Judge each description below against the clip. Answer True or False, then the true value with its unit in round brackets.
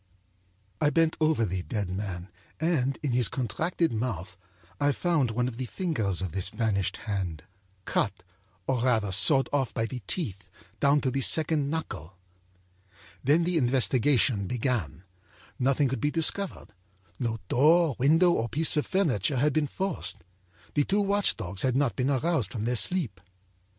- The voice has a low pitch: True (130 Hz)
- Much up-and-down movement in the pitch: True (6.4 semitones)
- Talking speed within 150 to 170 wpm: True (155 wpm)